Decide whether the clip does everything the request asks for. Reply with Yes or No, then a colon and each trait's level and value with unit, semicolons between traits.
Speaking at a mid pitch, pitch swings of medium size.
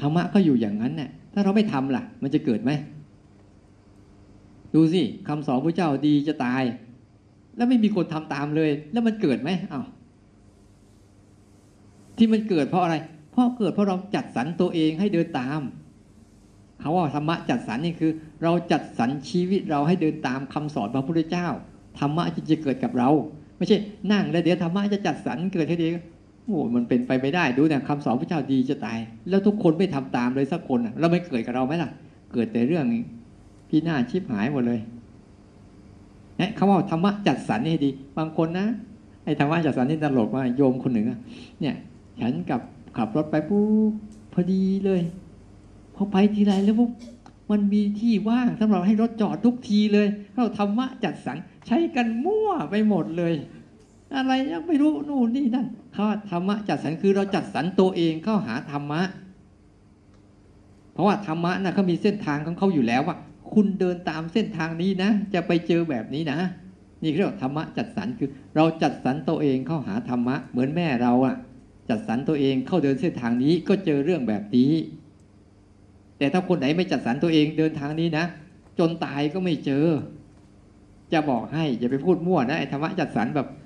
No: medium, 160 Hz; wide, 7.4 semitones